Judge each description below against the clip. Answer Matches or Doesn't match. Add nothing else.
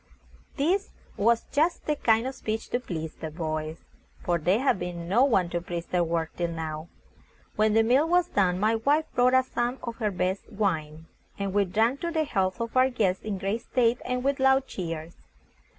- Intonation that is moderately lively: Doesn't match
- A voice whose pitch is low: Doesn't match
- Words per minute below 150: Doesn't match